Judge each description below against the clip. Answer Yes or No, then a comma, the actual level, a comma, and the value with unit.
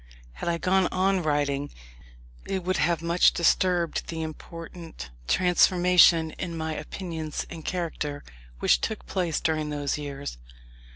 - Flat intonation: No, average, 3.0 semitones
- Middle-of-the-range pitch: Yes, medium, 165 Hz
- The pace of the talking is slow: Yes, slow, 130 wpm